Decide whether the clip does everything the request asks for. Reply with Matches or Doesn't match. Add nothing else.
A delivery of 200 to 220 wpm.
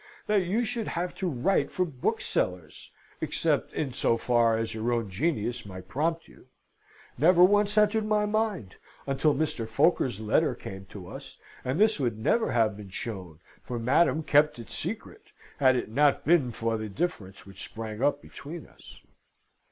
Doesn't match